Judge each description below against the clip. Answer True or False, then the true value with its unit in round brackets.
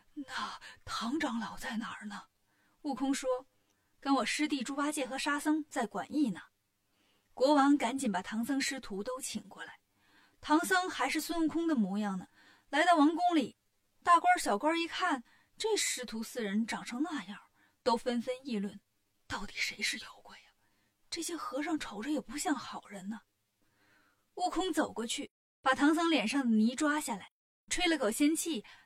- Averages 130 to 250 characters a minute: True (240 characters per minute)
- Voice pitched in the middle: False (255 Hz)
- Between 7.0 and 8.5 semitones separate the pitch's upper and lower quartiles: True (7.9 semitones)